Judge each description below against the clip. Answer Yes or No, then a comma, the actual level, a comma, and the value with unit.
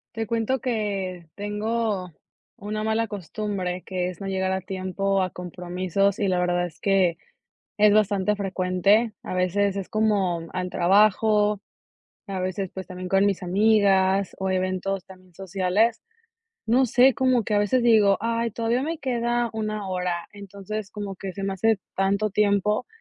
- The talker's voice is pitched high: Yes, high, 200 Hz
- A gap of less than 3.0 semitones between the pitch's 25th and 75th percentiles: Yes, narrow, 2.4 semitones